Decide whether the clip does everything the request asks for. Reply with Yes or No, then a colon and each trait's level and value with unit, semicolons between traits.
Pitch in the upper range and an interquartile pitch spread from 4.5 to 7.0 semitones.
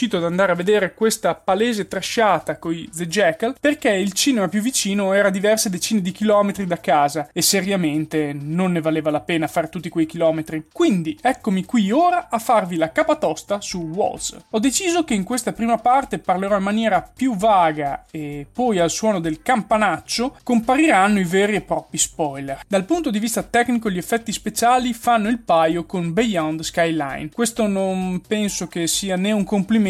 Yes: high, 200 Hz; average, 5.2 semitones